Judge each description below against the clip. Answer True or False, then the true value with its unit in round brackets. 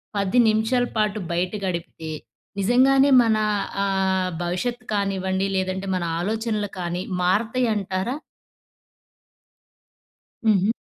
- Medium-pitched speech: False (200 Hz)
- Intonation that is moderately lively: True (3.0 semitones)